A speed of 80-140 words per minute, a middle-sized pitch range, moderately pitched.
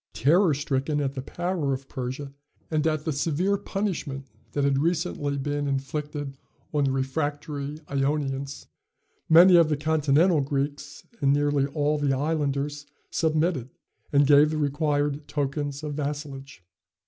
No: slow, 135 wpm; narrow, 1.8 semitones; medium, 145 Hz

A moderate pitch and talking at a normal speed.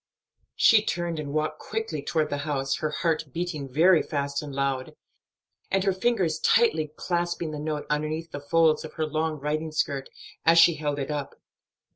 Yes: medium, 155 Hz; average, 175 wpm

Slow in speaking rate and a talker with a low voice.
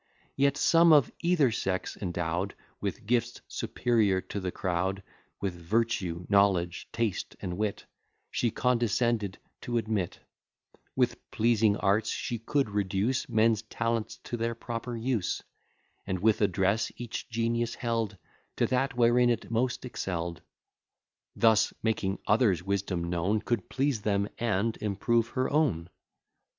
Yes: slow, 130 wpm; low, 110 Hz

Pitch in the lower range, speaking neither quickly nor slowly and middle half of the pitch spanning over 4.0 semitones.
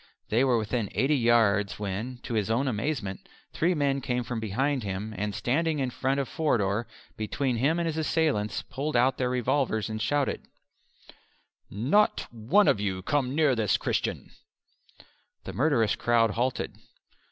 Yes: low, 125 Hz; average, 155 wpm; average, 4.4 semitones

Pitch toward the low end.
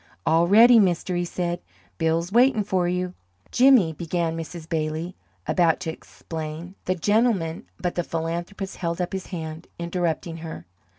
No: medium, 175 Hz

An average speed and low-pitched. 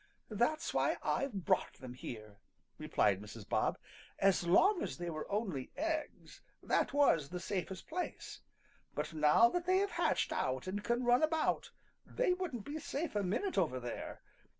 No: average, 165 wpm; high, 205 Hz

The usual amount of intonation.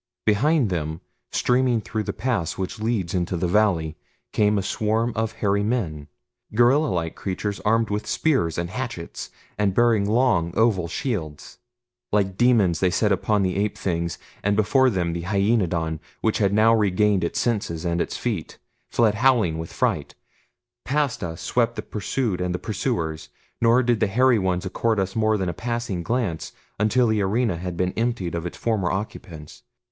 Yes: average, 4.5 semitones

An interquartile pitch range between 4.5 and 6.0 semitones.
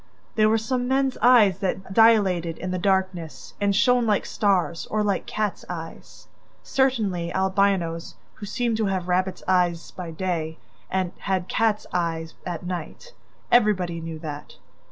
No: average, 3.8 semitones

